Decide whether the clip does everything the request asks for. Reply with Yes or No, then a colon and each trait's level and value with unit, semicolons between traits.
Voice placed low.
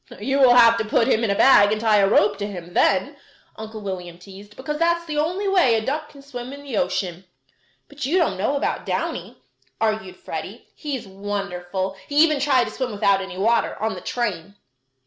No: high, 220 Hz